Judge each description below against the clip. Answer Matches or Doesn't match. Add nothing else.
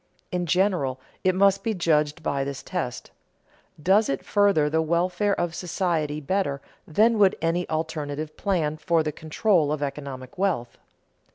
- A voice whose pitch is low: Doesn't match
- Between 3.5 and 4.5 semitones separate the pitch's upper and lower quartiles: Matches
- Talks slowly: Doesn't match